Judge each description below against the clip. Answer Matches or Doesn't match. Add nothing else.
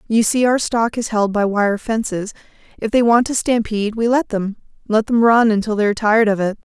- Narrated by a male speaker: Doesn't match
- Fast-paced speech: Matches